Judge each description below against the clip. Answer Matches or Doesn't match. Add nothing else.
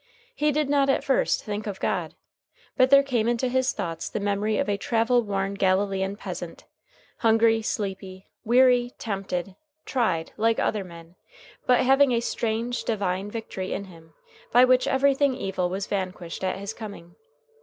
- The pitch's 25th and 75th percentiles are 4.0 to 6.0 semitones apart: Matches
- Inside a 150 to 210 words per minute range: Matches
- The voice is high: Matches